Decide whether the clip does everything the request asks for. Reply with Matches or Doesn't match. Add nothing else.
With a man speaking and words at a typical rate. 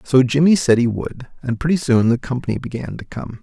Doesn't match